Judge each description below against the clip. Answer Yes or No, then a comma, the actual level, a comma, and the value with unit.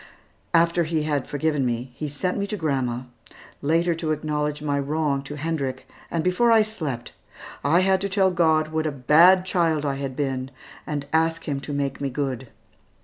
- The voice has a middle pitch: Yes, medium, 150 Hz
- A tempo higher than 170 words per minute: Yes, average, 185 wpm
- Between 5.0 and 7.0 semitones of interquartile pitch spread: No, average, 3.3 semitones